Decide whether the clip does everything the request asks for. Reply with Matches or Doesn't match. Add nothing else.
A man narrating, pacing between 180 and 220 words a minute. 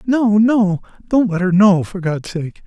Matches